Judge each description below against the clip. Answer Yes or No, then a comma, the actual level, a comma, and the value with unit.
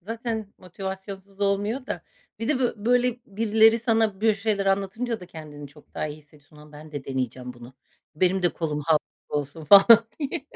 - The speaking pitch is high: Yes, high, 195 Hz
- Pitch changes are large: Yes, wide, 6.7 semitones